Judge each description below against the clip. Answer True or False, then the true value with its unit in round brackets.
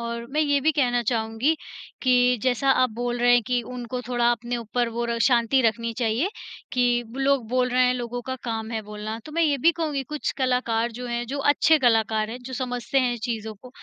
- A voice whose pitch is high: True (245 Hz)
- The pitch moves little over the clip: True (1.9 semitones)